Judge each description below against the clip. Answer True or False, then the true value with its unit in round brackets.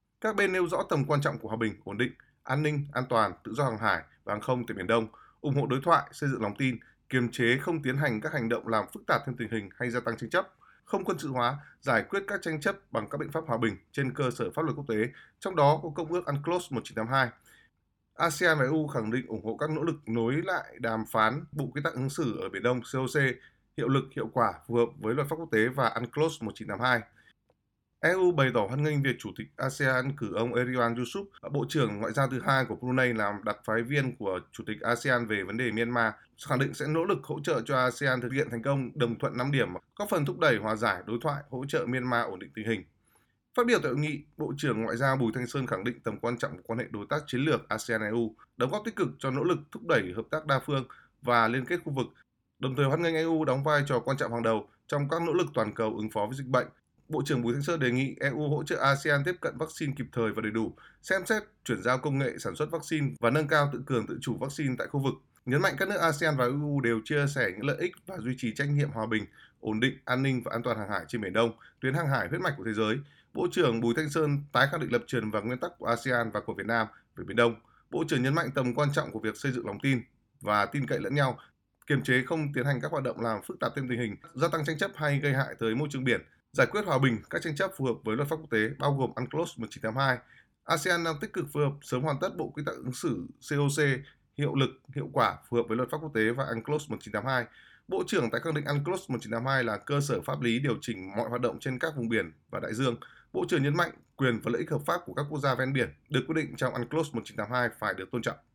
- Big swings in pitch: False (4.3 semitones)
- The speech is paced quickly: True (270 wpm)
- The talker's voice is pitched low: True (130 Hz)